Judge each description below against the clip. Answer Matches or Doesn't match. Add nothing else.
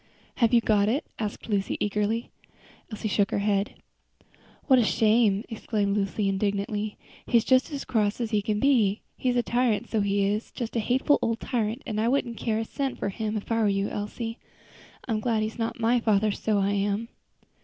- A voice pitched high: Matches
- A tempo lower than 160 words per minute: Doesn't match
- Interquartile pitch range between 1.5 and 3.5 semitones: Matches